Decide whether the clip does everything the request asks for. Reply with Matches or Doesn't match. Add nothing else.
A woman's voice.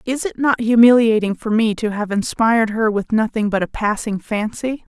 Matches